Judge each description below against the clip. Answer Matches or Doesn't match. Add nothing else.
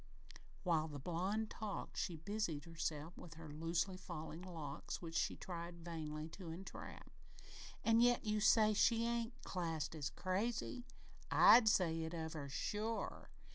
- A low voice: Doesn't match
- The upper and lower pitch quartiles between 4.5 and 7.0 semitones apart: Matches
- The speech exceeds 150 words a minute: Doesn't match